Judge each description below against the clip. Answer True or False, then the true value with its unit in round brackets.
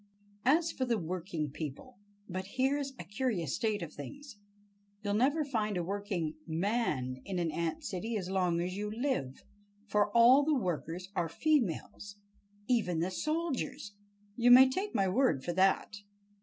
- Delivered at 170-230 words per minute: False (155 wpm)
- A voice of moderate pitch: False (205 Hz)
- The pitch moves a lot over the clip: True (6.4 semitones)